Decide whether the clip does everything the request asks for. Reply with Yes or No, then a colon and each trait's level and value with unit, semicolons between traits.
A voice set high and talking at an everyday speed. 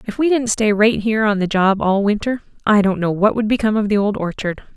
No: high, 210 Hz; fast, 265 wpm